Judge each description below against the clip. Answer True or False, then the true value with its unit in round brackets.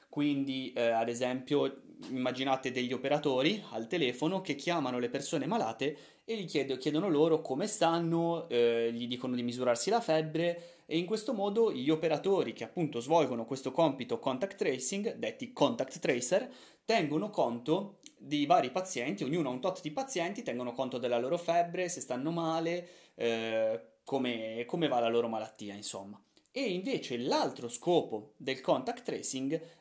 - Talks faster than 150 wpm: True (160 wpm)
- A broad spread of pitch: True (5.9 semitones)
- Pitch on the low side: False (145 Hz)